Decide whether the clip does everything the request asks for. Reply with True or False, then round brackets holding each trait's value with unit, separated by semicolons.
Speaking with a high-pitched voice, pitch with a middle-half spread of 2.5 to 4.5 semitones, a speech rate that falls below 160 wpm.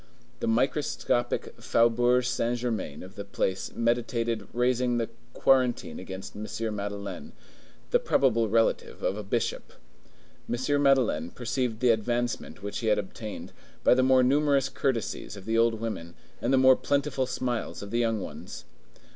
False (115 Hz; 2.9 semitones; 150 wpm)